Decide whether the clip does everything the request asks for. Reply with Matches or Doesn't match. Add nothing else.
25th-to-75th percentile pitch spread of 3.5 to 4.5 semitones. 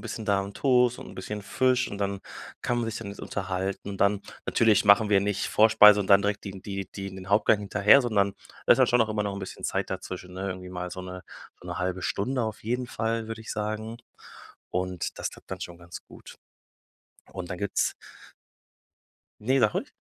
Doesn't match